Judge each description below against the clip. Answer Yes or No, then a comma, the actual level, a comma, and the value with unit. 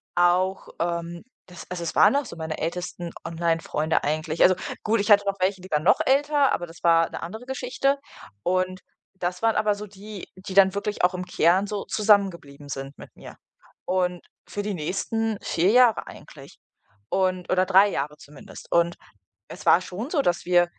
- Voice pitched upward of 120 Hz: Yes, medium, 185 Hz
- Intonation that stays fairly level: No, average, 3.2 semitones